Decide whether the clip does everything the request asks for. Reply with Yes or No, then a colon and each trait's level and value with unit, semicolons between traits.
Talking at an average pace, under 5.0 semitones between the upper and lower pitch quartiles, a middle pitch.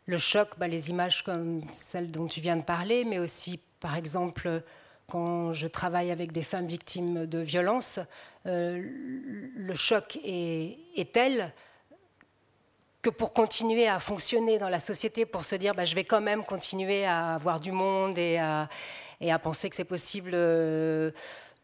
Yes: average, 170 wpm; average, 3.4 semitones; medium, 180 Hz